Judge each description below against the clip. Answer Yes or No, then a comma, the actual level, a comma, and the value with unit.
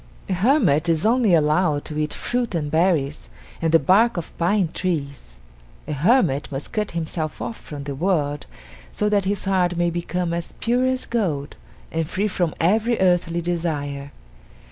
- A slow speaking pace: No, average, 165 wpm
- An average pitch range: Yes, average, 4.8 semitones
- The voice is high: No, medium, 170 Hz